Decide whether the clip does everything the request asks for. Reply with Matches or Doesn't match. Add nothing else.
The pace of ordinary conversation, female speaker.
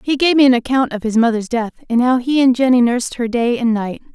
Doesn't match